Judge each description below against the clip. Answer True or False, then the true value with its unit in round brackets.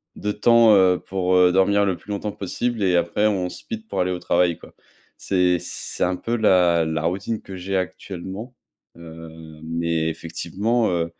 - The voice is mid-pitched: False (90 Hz)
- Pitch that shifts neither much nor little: True (3.2 semitones)